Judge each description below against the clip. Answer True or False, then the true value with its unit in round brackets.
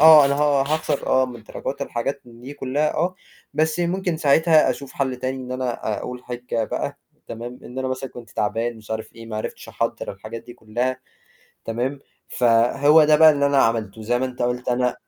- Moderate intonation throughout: True (3.3 semitones)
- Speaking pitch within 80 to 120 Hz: False (130 Hz)